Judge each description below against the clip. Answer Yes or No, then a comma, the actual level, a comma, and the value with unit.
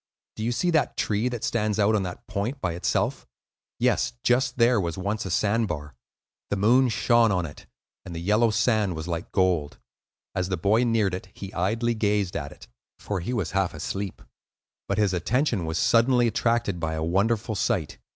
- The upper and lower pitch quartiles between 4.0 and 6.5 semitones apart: Yes, average, 4.3 semitones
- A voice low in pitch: Yes, low, 105 Hz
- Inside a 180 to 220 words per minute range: Yes, average, 190 wpm